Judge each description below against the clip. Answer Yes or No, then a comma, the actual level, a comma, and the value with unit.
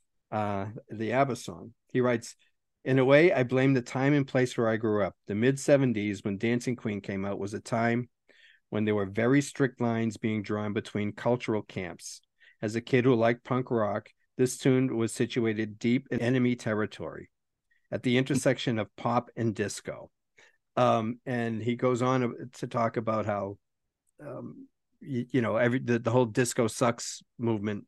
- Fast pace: No, average, 180 wpm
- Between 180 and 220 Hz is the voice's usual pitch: No, low, 120 Hz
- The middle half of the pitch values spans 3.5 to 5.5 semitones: No, average, 2.8 semitones